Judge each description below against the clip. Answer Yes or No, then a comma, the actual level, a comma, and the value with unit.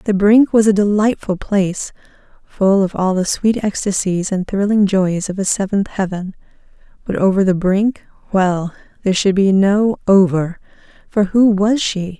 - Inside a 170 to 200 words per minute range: No, average, 155 wpm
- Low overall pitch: No, high, 195 Hz